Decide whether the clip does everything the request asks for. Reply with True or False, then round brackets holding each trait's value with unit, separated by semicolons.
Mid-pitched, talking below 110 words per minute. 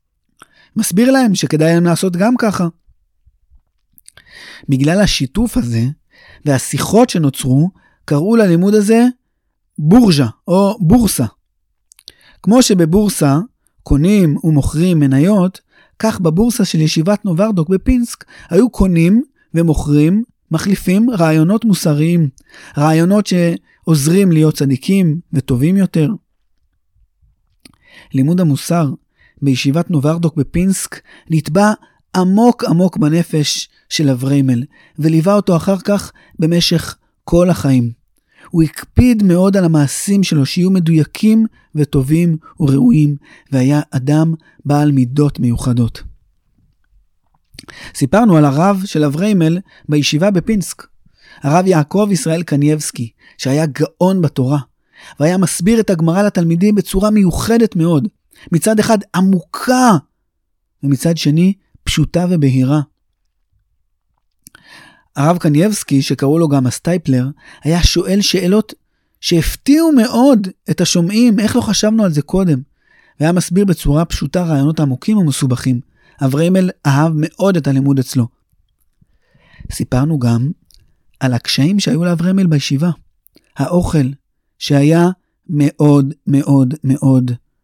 True (165 Hz; 100 wpm)